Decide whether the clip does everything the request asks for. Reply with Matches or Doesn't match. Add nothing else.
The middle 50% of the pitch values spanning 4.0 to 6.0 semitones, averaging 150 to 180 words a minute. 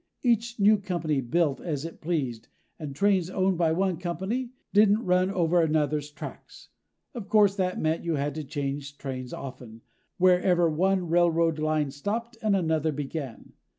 Matches